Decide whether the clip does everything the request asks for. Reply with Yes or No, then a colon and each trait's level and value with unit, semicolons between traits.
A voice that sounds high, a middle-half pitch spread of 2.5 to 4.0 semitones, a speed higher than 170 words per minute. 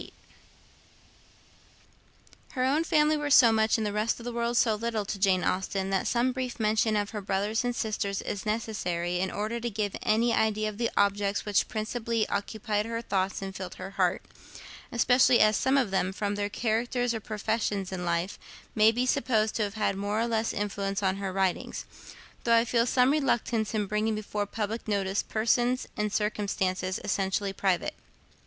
Yes: high, 215 Hz; average, 2.8 semitones; average, 180 wpm